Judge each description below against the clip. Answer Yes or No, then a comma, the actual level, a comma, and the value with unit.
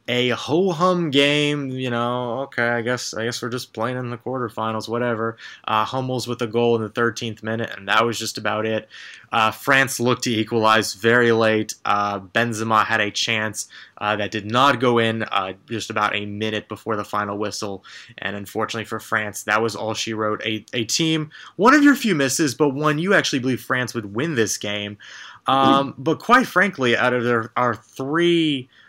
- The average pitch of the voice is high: No, low, 115 Hz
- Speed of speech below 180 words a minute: No, average, 200 wpm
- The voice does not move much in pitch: No, average, 3.2 semitones